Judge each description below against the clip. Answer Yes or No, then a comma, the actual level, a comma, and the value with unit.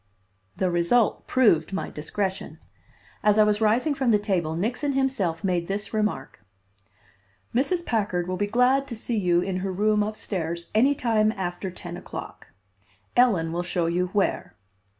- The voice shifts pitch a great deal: No, average, 4.4 semitones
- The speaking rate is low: No, average, 160 wpm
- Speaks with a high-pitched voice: Yes, high, 205 Hz